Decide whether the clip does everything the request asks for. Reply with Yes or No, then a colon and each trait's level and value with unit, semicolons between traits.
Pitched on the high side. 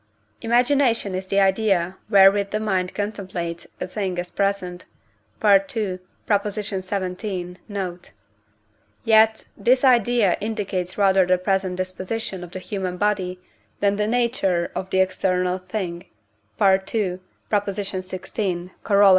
Yes: high, 195 Hz